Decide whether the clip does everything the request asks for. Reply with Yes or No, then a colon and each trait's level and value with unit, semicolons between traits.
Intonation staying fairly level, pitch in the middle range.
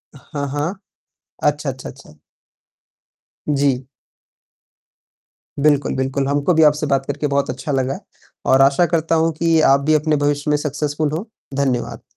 Yes: narrow, 1.9 semitones; medium, 145 Hz